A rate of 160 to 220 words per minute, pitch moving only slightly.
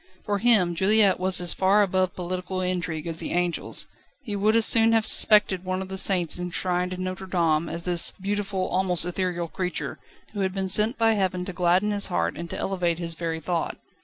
Yes: fast, 205 wpm; narrow, 2.1 semitones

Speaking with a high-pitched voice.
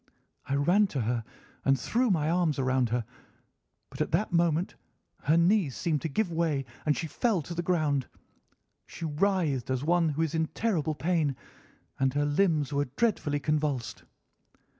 No: medium, 155 Hz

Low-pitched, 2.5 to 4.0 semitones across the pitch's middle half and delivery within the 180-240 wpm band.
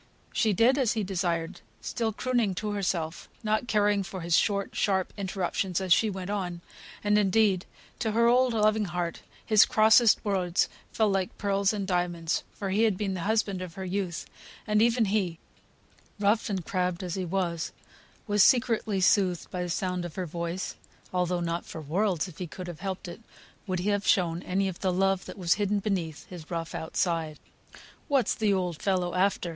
No: high, 190 Hz; average, 2.9 semitones; average, 185 wpm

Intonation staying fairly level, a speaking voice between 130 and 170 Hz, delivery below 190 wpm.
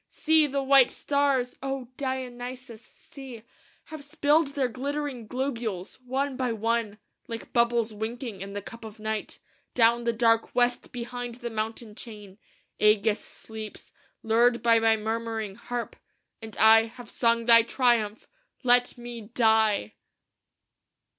No: narrow, 2.3 semitones; high, 235 Hz; slow, 135 wpm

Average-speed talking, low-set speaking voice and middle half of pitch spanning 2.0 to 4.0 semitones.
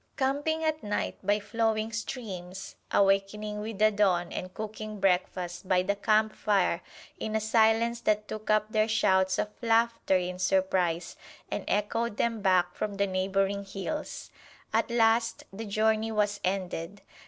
No: average, 145 wpm; high, 210 Hz; narrow, 2.6 semitones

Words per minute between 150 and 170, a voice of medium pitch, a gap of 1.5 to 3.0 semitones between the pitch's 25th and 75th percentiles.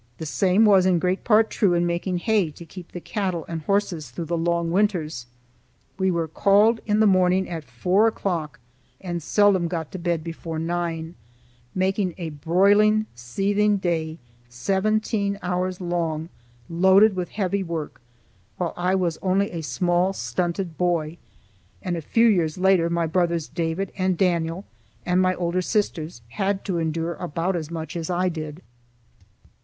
Yes: average, 160 wpm; medium, 175 Hz; narrow, 2.6 semitones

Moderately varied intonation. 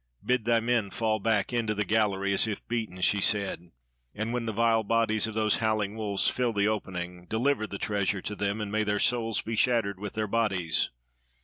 No: narrow, 2.1 semitones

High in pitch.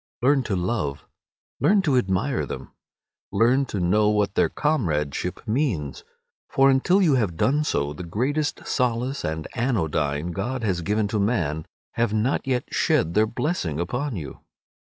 No: low, 110 Hz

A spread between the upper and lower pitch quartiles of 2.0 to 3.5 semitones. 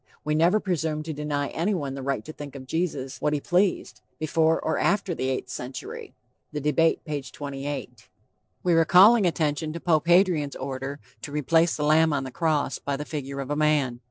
Yes: average, 2.8 semitones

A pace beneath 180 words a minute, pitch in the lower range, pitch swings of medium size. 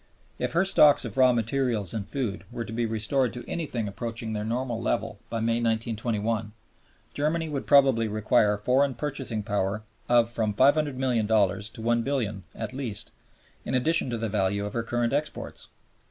Yes: average, 165 wpm; low, 115 Hz; average, 3.4 semitones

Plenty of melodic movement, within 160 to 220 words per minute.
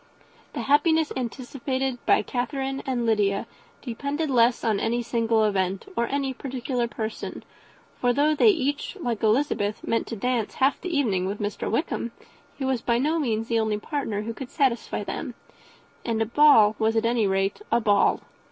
No: average, 3.7 semitones; average, 170 wpm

